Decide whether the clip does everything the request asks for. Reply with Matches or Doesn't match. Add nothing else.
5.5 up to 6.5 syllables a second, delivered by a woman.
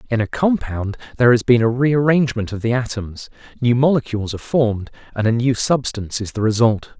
Doesn't match